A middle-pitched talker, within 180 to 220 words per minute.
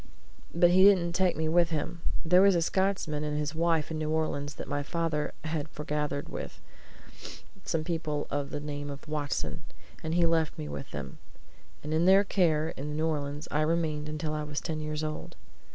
Yes: medium, 155 Hz; average, 195 wpm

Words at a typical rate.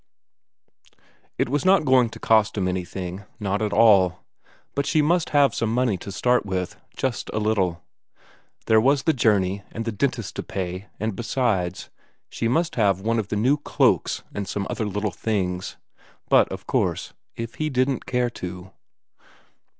Yes: average, 165 wpm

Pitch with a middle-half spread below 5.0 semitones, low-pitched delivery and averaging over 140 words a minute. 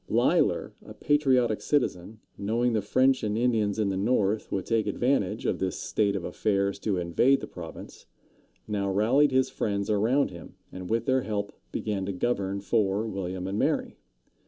Yes: average, 3.4 semitones; low, 105 Hz; average, 170 wpm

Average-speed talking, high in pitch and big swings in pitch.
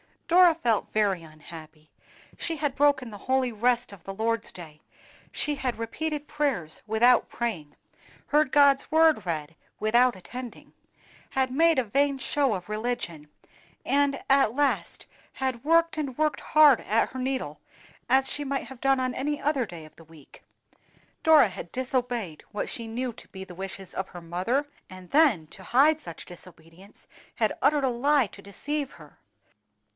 Yes: average, 165 wpm; high, 245 Hz; wide, 6.6 semitones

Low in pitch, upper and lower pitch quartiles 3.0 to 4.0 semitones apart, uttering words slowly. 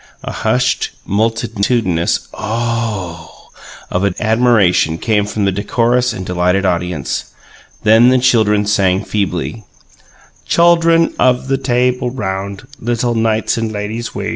Yes: low, 110 Hz; average, 3.7 semitones; slow, 125 wpm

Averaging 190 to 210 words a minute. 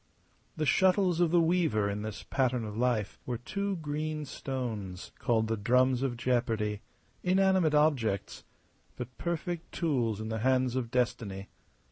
No: average, 145 wpm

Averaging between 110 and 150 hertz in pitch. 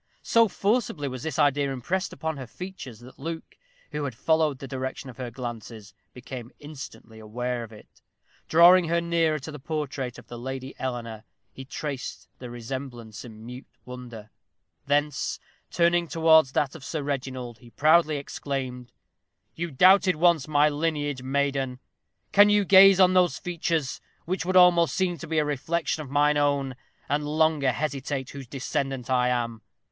Yes: medium, 140 Hz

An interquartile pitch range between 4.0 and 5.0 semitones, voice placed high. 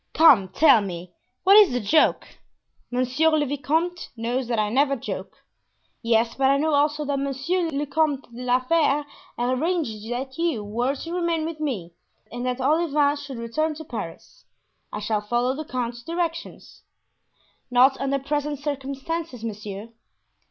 Yes: average, 4.5 semitones; very high, 275 Hz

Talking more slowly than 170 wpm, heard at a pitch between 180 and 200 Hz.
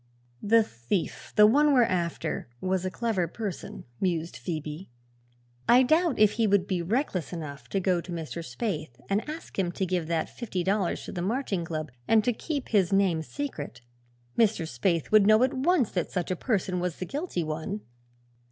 No: average, 185 wpm; high, 190 Hz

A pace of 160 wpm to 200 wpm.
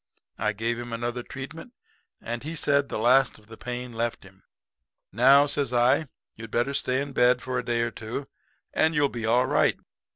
Yes: average, 195 wpm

